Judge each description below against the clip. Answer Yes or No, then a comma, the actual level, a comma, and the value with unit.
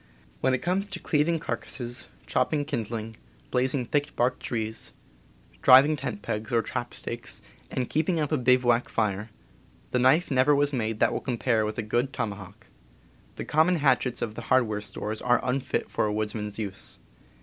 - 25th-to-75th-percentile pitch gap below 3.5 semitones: No, average, 4.1 semitones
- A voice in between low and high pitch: No, low, 120 Hz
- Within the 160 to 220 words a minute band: Yes, average, 175 wpm